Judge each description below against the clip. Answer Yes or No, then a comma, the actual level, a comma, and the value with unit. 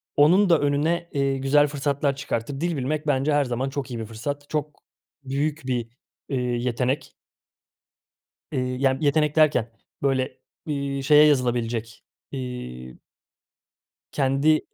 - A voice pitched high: No, medium, 140 Hz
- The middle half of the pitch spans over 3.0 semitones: No, average, 2.7 semitones